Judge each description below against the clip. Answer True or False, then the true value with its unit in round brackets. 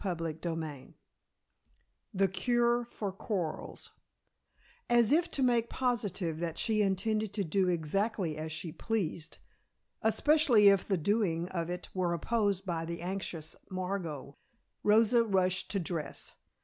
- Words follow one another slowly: True (130 wpm)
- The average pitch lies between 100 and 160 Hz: False (190 Hz)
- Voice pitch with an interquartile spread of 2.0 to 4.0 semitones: False (4.7 semitones)